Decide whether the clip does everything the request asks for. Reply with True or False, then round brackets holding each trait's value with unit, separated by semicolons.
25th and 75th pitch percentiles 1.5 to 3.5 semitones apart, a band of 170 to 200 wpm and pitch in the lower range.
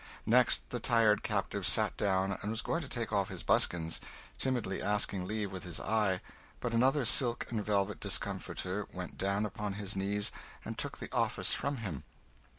True (3.1 semitones; 175 wpm; 105 Hz)